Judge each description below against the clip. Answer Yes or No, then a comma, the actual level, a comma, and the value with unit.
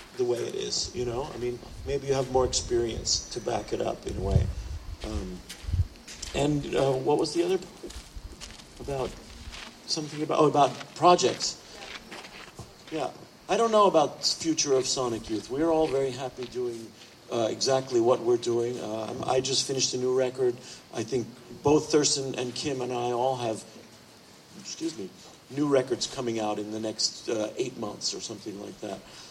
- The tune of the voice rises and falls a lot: No, average, 4.3 semitones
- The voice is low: Yes, low, 130 Hz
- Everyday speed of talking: No, fast, 180 wpm